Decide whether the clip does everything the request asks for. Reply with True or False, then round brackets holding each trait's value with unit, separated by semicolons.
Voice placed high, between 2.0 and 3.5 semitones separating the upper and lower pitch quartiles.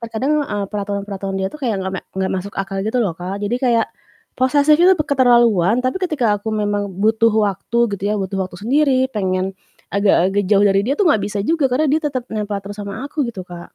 False (210 Hz; 4.7 semitones)